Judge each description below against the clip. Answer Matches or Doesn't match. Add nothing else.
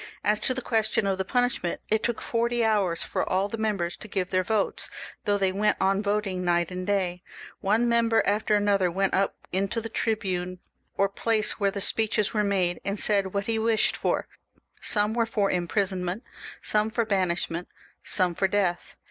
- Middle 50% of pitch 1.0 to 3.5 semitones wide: Matches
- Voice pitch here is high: Matches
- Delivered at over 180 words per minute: Matches